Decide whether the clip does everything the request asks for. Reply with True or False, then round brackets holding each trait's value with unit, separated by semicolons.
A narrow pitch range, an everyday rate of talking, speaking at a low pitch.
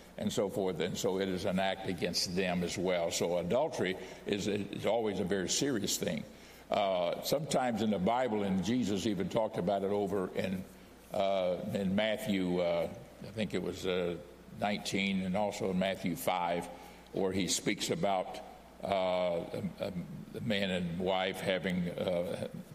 True (1.5 semitones; 165 wpm; 95 Hz)